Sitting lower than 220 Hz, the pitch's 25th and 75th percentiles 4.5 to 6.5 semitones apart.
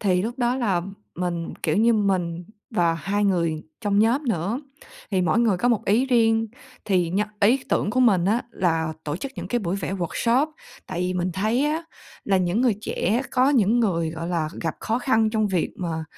Yes: high, 200 Hz; average, 5.1 semitones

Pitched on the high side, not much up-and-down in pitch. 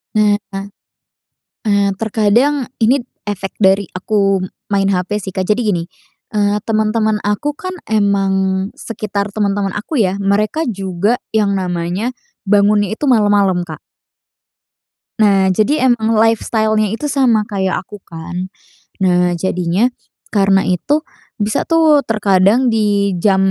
Yes: high, 205 Hz; narrow, 2.3 semitones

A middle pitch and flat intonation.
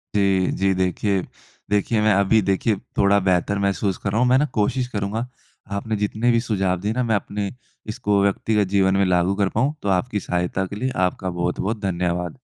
No: low, 100 Hz; narrow, 2.3 semitones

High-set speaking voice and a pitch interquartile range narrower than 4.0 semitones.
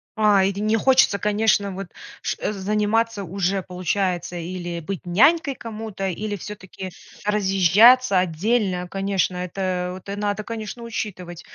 Yes: high, 200 Hz; average, 2.7 semitones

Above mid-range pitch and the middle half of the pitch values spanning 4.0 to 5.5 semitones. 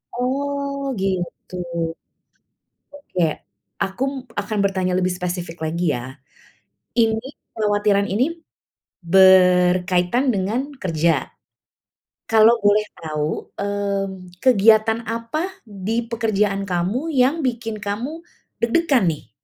Yes: high, 205 Hz; average, 4.7 semitones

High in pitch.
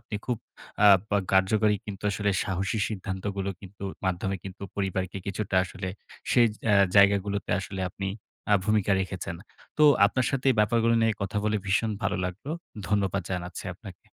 No: low, 100 Hz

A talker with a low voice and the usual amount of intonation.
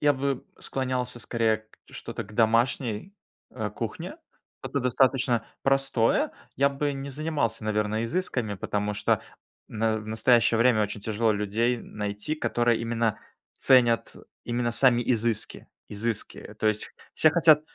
Yes: low, 115 Hz; average, 3.4 semitones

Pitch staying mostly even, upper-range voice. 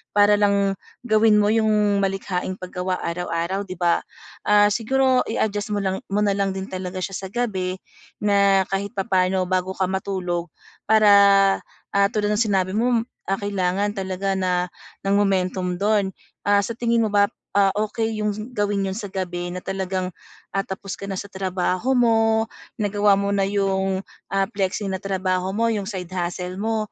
Yes: narrow, 1.8 semitones; high, 195 Hz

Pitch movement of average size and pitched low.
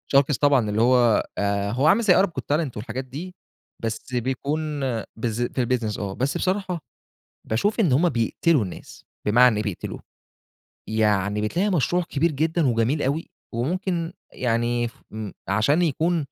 No: wide, 6.7 semitones; low, 130 Hz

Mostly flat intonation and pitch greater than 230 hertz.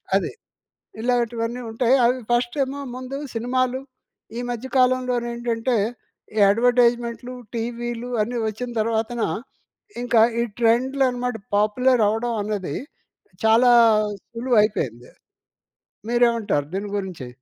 Yes: narrow, 1.9 semitones; high, 240 Hz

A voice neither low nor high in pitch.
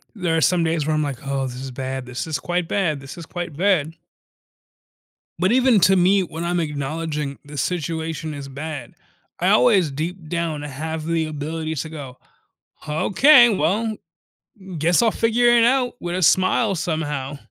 Yes: medium, 160 Hz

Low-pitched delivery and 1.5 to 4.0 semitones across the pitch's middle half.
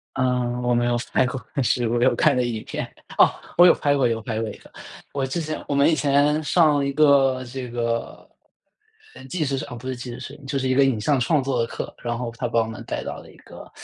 Yes: low, 130 Hz; average, 2.8 semitones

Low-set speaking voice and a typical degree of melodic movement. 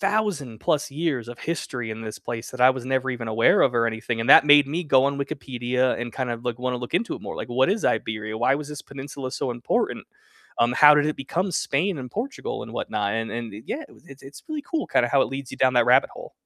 Yes: low, 130 Hz; average, 3.7 semitones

